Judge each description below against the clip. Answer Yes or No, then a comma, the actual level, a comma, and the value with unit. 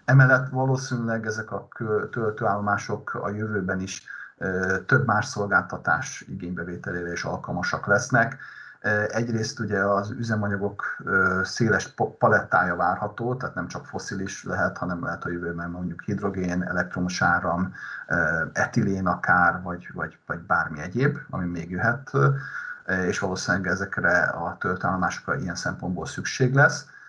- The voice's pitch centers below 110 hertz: Yes, low, 100 Hz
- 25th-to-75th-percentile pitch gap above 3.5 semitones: Yes, average, 4.6 semitones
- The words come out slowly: No, average, 120 wpm